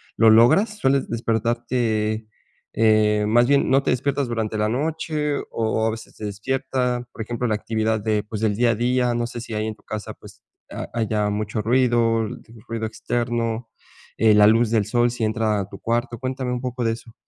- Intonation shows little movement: Yes, narrow, 2.2 semitones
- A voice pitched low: Yes, low, 115 Hz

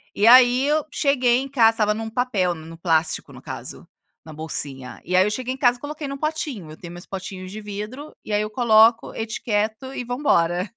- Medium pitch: No, high, 220 Hz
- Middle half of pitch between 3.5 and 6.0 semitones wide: Yes, wide, 5.6 semitones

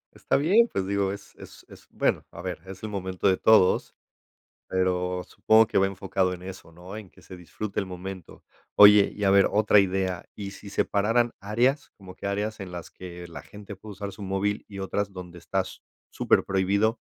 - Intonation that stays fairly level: Yes, narrow, 1.9 semitones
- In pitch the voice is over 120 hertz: No, very low, 95 Hz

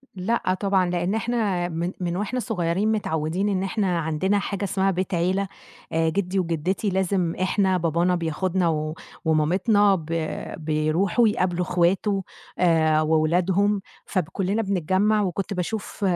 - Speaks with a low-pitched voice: No, medium, 185 Hz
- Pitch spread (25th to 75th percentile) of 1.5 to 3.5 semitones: Yes, average, 2.8 semitones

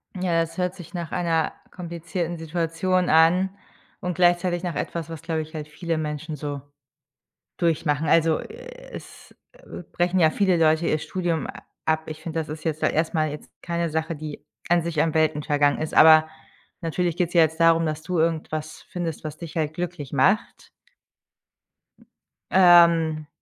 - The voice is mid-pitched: Yes, medium, 165 Hz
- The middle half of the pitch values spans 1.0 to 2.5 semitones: Yes, narrow, 2.0 semitones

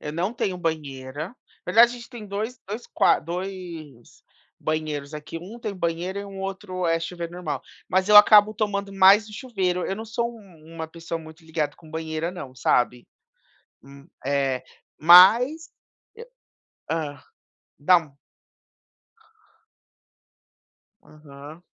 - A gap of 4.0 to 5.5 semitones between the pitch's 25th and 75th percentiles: Yes, average, 4.4 semitones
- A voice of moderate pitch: Yes, medium, 175 Hz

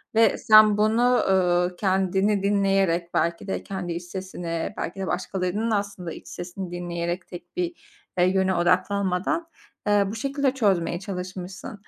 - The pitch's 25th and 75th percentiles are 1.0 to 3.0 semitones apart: Yes, narrow, 2.6 semitones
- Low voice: No, high, 190 Hz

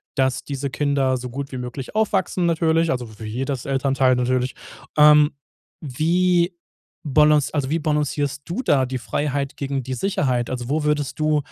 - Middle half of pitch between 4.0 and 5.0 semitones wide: No, average, 2.8 semitones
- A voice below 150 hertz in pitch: Yes, medium, 140 Hz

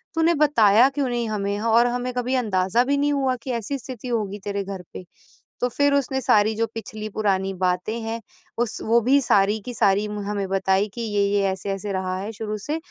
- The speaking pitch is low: No, high, 220 Hz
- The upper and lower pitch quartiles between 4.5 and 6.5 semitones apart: No, average, 3.7 semitones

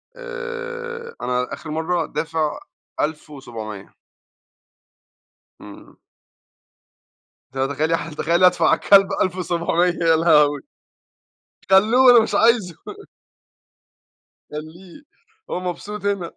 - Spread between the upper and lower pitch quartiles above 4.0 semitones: Yes, wide, 5.4 semitones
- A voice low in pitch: No, medium, 175 Hz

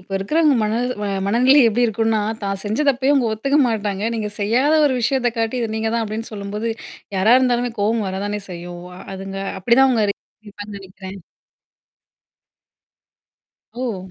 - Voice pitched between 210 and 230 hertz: Yes, high, 220 Hz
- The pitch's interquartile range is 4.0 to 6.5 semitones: No, average, 3.5 semitones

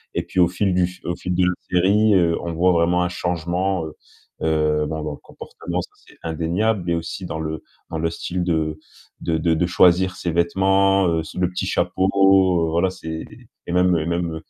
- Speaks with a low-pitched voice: Yes, very low, 85 Hz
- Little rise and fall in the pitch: Yes, narrow, 2.1 semitones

